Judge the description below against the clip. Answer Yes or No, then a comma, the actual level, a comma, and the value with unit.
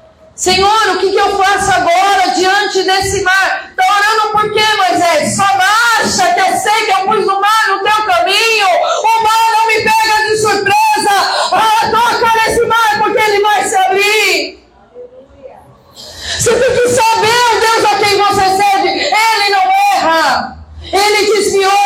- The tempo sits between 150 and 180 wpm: Yes, average, 160 wpm